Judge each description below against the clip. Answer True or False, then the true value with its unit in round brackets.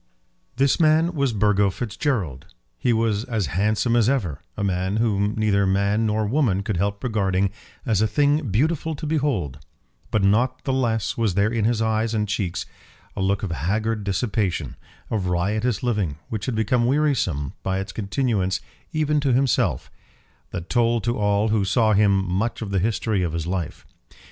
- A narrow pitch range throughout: False (3.6 semitones)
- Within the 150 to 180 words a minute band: True (175 wpm)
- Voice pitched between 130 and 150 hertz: False (105 Hz)